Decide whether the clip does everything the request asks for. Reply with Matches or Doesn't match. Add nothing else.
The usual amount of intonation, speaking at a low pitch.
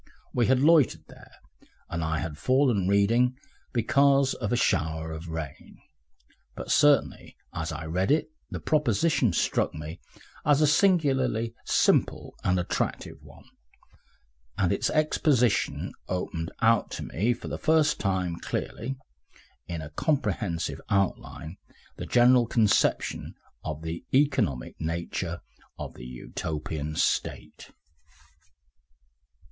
Doesn't match